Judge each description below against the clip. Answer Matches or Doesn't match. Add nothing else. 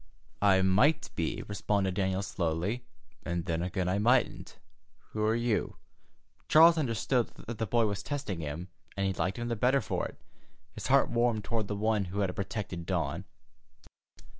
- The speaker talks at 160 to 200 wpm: Matches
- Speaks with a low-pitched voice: Matches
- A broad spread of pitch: Doesn't match